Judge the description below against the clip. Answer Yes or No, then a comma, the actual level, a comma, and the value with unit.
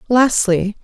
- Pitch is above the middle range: Yes, high, 215 Hz